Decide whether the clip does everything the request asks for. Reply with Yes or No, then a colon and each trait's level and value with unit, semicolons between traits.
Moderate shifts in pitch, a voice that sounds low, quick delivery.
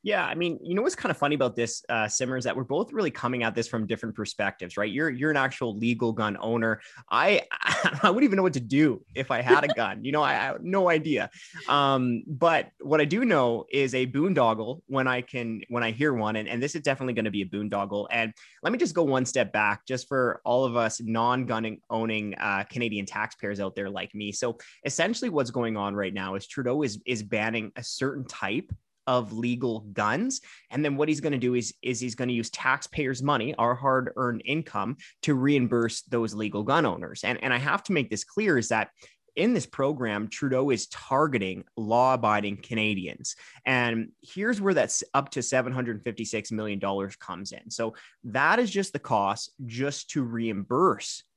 Yes: average, 4.2 semitones; low, 125 Hz; fast, 215 wpm